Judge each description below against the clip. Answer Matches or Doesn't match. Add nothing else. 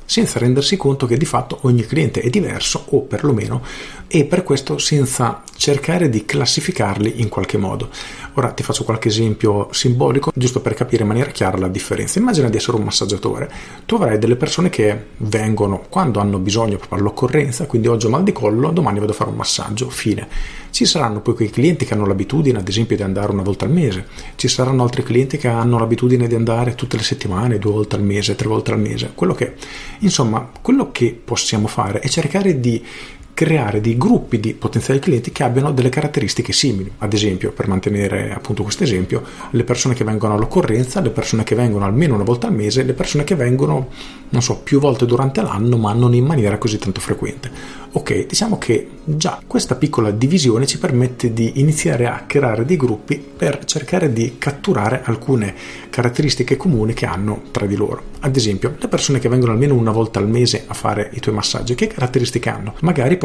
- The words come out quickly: Matches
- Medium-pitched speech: Doesn't match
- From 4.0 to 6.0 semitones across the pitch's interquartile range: Matches